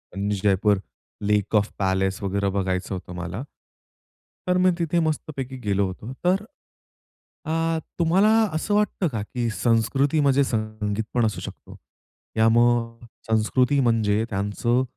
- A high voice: No, low, 115 Hz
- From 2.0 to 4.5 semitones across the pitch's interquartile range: No, wide, 5.4 semitones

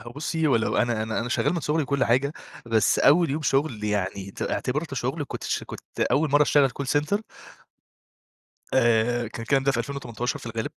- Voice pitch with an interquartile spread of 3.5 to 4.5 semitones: Yes, average, 4.1 semitones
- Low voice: Yes, low, 130 Hz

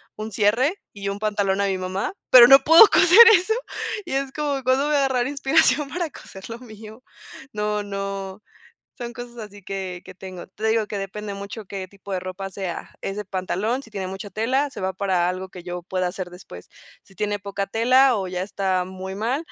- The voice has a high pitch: Yes, high, 205 Hz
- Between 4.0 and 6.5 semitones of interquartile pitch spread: Yes, average, 4.3 semitones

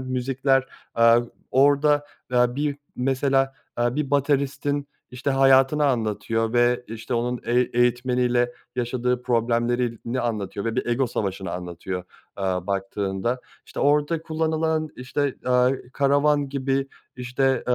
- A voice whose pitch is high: No, low, 125 Hz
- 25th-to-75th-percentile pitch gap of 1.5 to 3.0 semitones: Yes, average, 2.7 semitones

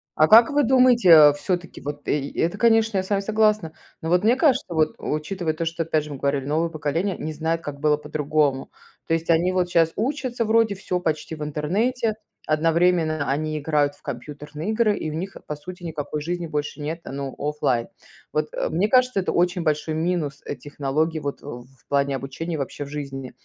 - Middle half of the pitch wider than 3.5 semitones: Yes, average, 4.1 semitones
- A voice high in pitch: No, medium, 160 Hz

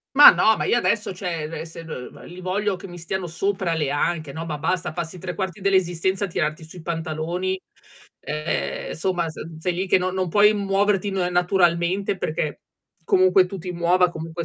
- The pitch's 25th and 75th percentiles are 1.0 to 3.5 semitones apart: Yes, narrow, 2.4 semitones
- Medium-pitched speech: Yes, medium, 180 Hz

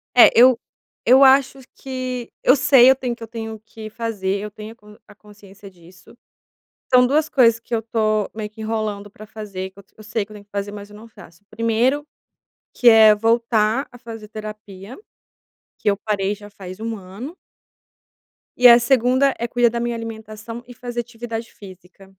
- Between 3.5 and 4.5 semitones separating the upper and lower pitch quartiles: No, narrow, 2.5 semitones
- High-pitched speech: Yes, high, 220 Hz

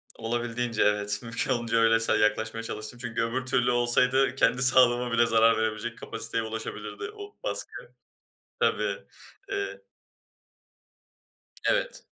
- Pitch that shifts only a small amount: Yes, narrow, 1.8 semitones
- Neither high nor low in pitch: No, low, 115 Hz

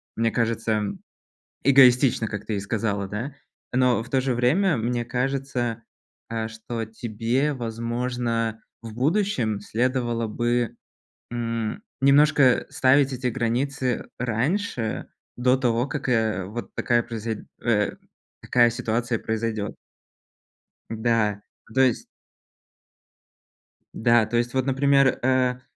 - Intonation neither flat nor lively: No, narrow, 2.3 semitones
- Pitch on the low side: Yes, low, 120 Hz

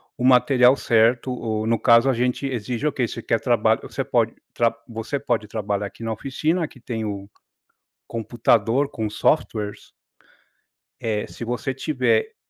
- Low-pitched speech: Yes, low, 120 Hz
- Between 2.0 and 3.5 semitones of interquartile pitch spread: Yes, average, 2.7 semitones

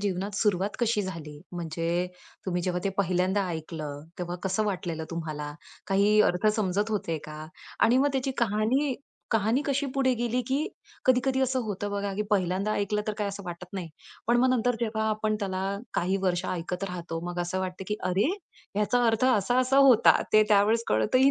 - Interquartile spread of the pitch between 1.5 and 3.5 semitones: No, average, 4.3 semitones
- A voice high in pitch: Yes, high, 200 Hz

